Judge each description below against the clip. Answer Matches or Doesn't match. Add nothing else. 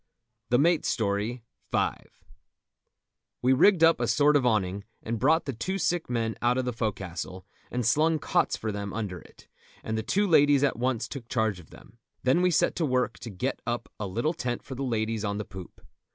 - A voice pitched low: Matches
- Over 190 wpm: Matches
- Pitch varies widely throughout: Doesn't match